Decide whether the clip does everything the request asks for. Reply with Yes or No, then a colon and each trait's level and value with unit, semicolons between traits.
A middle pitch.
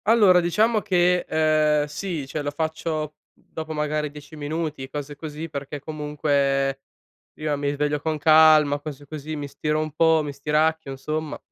Yes: medium, 150 Hz